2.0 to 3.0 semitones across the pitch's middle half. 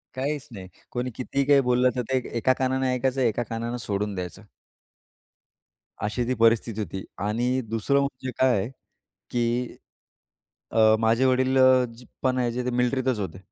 Yes: narrow, 2.4 semitones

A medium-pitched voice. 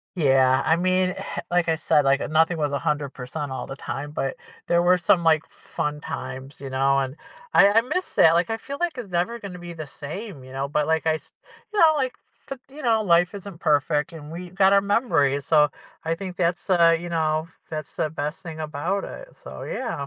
Yes: medium, 165 Hz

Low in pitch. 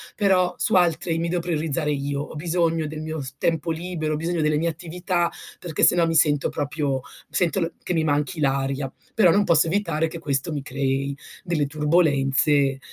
No: medium, 160 Hz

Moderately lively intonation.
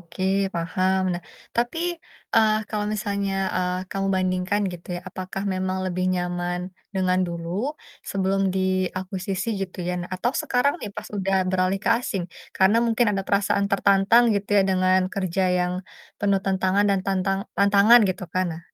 No: narrow, 1.6 semitones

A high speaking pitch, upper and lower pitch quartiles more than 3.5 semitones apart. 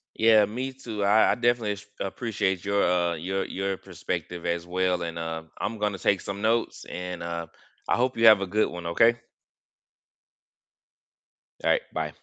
No: low, 100 Hz; average, 4.1 semitones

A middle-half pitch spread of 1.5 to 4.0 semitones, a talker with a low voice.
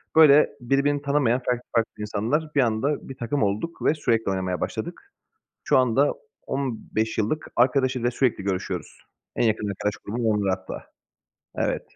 No: average, 4.7 semitones; low, 120 Hz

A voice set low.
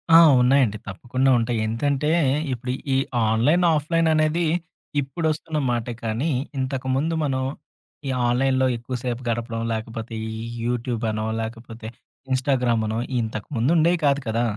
Yes: low, 125 Hz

